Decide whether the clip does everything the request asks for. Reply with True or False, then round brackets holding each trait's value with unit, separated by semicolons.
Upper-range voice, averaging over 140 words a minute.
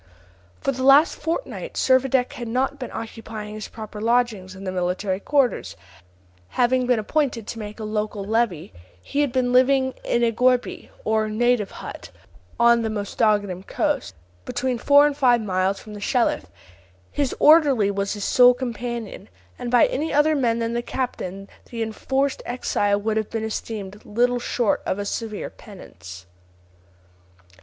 True (230 Hz; 160 wpm)